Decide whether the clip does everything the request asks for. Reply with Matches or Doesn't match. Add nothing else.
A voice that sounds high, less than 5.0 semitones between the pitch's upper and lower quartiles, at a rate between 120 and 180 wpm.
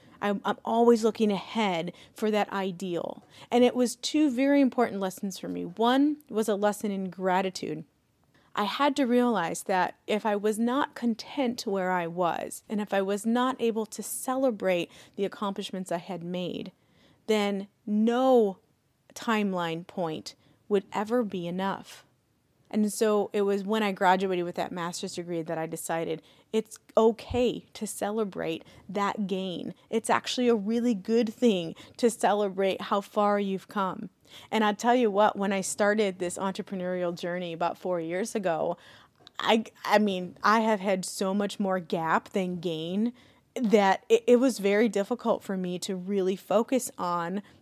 Matches